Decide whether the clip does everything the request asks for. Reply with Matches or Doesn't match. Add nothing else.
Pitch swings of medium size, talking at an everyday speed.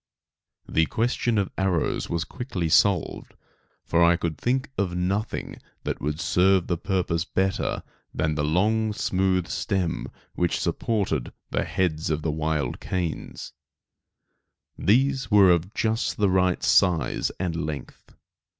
Doesn't match